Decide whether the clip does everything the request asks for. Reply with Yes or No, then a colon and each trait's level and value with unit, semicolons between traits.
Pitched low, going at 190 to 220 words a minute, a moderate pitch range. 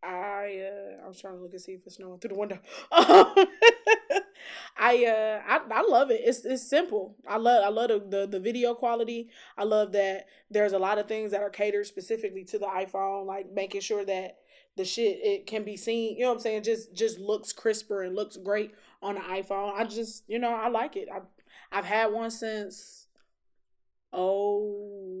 No: high, 210 Hz; average, 200 wpm; average, 3.0 semitones